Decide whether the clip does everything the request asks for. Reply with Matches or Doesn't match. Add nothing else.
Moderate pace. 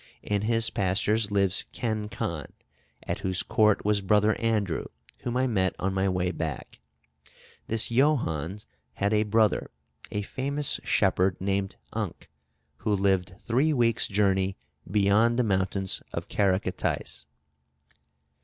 Doesn't match